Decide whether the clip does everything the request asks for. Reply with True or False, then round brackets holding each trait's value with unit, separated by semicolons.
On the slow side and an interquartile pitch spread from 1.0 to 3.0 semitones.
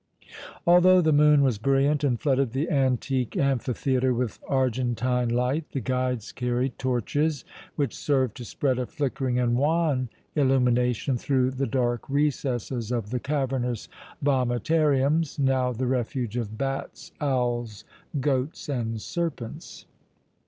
True (125 wpm; 2.4 semitones)